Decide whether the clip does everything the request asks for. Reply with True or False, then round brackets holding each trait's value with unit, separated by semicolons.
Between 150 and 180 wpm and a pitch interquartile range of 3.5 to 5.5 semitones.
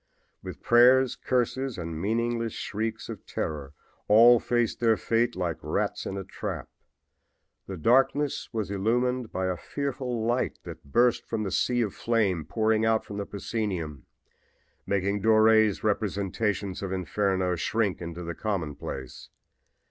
False (140 wpm; 3.9 semitones)